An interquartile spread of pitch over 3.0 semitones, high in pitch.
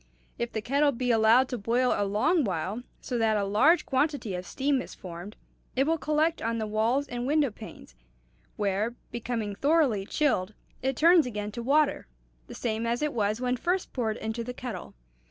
Yes: average, 4.7 semitones; high, 235 Hz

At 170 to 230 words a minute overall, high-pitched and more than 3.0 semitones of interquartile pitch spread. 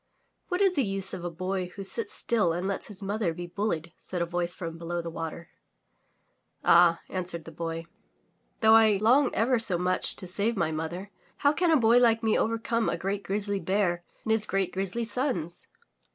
Yes: average, 195 wpm; high, 195 Hz; average, 4.4 semitones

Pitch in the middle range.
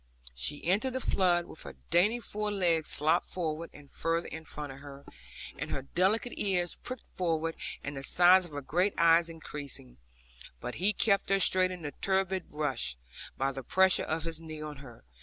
Yes: medium, 165 Hz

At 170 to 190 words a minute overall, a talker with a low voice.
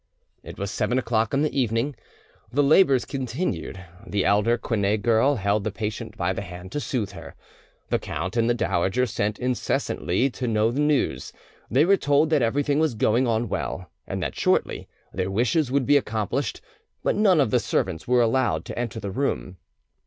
Yes: average, 185 wpm; low, 115 Hz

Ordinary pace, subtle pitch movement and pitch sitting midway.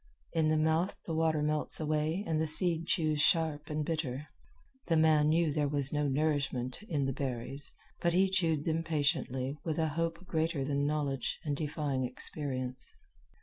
Yes: average, 170 wpm; narrow, 2.2 semitones; medium, 155 Hz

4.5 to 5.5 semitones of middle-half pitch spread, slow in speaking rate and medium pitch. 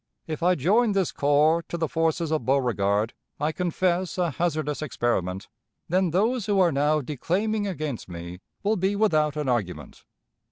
No: average, 5.1 semitones; average, 160 wpm; medium, 155 Hz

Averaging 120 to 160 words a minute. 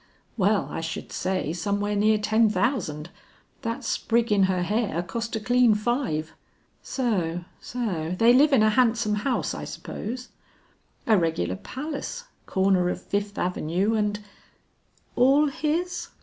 Yes: average, 145 wpm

